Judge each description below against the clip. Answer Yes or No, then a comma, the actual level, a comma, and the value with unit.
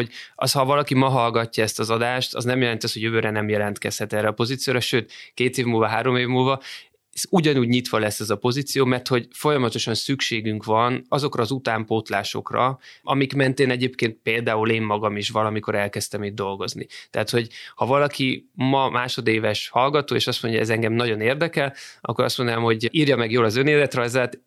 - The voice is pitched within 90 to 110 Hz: No, low, 120 Hz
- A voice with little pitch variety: No, average, 3.1 semitones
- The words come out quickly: Yes, fast, 190 wpm